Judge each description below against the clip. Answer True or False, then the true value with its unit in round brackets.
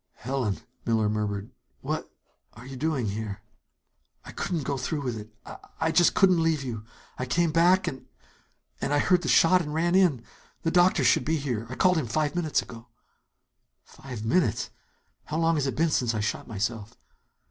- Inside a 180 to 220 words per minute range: True (185 wpm)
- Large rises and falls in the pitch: True (6.3 semitones)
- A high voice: False (135 Hz)